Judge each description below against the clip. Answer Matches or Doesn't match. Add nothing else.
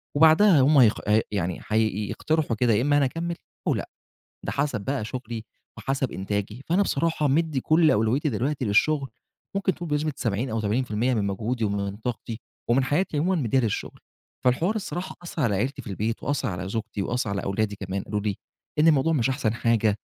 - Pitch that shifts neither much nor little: Doesn't match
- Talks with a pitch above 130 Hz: Doesn't match